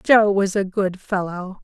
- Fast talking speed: No, average, 185 wpm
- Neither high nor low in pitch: No, high, 195 Hz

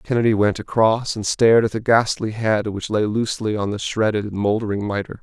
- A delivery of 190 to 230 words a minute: Yes, fast, 205 wpm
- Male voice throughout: Yes, male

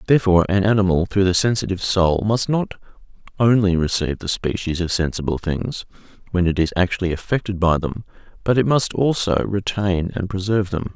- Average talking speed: Yes, average, 170 wpm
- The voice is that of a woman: No, male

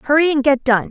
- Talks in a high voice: Yes, very high, 275 Hz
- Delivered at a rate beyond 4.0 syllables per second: Yes, 5.8 syllables/s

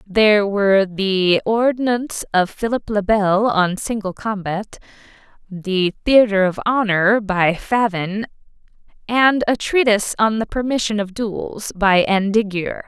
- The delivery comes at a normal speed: No, slow, 125 wpm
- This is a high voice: Yes, high, 205 Hz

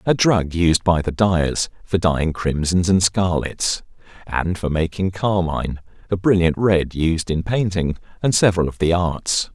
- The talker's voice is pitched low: Yes, very low, 90 Hz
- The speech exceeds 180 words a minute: No, average, 165 wpm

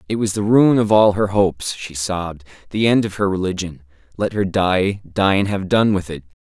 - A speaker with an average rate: No, fast, 225 wpm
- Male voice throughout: Yes, male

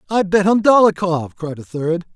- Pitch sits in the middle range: Yes, medium, 180 Hz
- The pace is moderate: Yes, average, 195 wpm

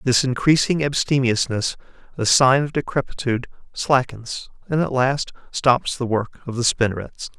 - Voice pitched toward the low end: Yes, low, 130 Hz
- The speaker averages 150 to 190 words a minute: No, average, 140 wpm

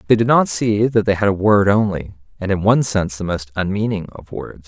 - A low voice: Yes, low, 100 Hz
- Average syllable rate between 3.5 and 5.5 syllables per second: No, 5.8 syllables/s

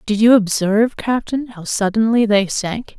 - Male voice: No, female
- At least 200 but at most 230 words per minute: No, average, 160 wpm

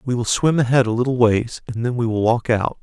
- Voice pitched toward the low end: Yes, low, 120 Hz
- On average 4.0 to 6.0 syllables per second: Yes, 5.8 syllables/s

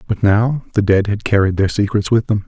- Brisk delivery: Yes, fast, 245 wpm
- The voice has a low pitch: Yes, low, 105 Hz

